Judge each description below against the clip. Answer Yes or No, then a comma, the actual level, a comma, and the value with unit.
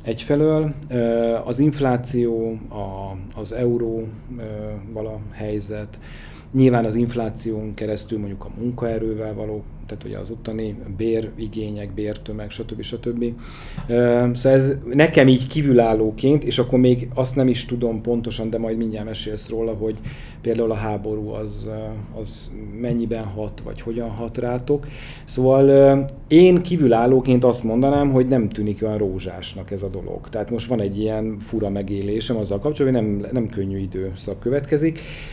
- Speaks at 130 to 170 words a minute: Yes, average, 140 wpm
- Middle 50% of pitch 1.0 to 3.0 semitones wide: Yes, average, 2.7 semitones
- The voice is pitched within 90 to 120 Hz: Yes, low, 115 Hz